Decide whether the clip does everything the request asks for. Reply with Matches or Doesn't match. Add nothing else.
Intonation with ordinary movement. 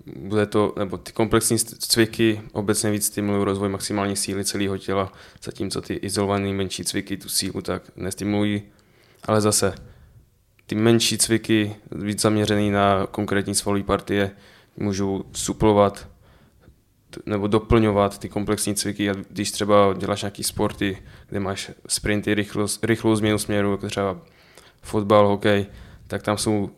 Doesn't match